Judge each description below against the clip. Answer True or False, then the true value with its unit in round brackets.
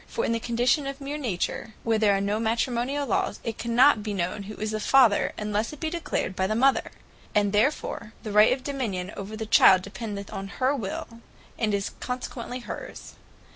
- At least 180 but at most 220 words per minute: True (200 wpm)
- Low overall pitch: False (225 Hz)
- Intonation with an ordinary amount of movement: True (3.7 semitones)